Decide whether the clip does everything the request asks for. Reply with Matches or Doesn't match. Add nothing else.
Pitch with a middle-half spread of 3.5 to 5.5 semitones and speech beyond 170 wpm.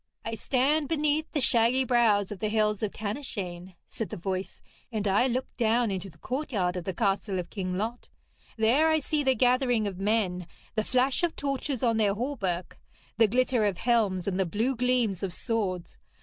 Matches